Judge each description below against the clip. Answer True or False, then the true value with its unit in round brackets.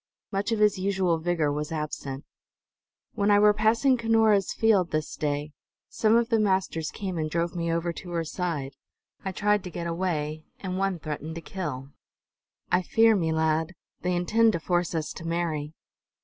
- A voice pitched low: False (175 Hz)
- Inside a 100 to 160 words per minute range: False (175 wpm)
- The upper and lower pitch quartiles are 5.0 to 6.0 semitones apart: False (4.1 semitones)